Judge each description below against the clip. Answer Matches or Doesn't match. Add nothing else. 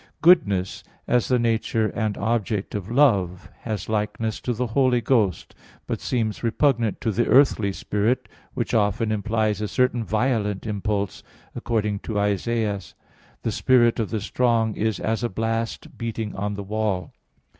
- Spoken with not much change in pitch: Matches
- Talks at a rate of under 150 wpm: Doesn't match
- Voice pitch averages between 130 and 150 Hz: Doesn't match